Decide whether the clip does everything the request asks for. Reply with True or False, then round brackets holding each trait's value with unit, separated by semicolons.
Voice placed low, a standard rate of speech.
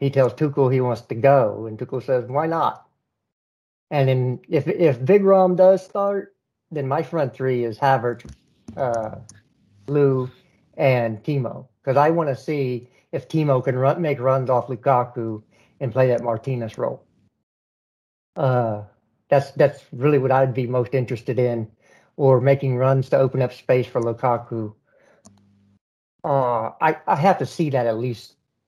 True (130 Hz; 160 wpm)